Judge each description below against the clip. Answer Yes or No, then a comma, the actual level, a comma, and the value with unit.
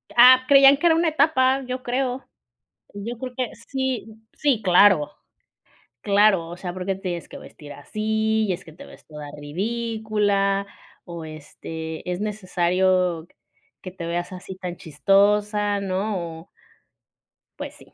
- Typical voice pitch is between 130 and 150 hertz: No, high, 200 Hz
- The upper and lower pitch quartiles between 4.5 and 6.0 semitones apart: Yes, average, 5.1 semitones